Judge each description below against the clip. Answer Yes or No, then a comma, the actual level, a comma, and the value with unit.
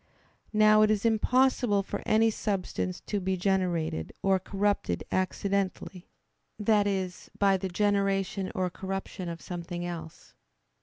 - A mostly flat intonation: Yes, narrow, 2.3 semitones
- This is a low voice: No, high, 195 Hz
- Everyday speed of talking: No, slow, 130 wpm